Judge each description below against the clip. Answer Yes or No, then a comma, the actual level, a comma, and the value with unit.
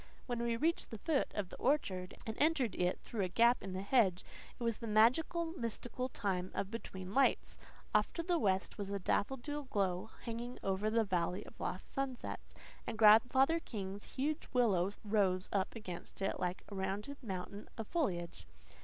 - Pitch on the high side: Yes, high, 215 Hz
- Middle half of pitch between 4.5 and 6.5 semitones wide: Yes, average, 4.9 semitones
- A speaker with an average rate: Yes, average, 180 wpm